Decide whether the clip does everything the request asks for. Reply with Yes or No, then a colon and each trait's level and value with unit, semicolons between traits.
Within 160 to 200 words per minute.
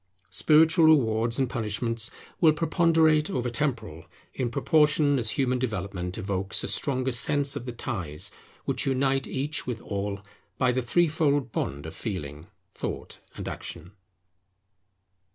No: slow, 135 wpm